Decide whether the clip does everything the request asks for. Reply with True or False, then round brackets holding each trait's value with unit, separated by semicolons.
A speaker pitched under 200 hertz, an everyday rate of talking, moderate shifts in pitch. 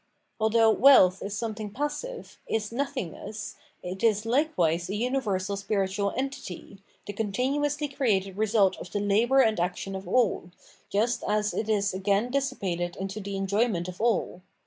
False (210 Hz; 150 wpm; 3.8 semitones)